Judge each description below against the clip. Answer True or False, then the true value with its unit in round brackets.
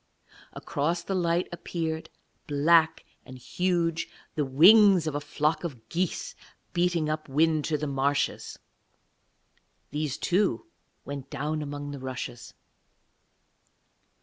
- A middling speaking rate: False (115 wpm)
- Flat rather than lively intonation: False (3.1 semitones)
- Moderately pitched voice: True (155 Hz)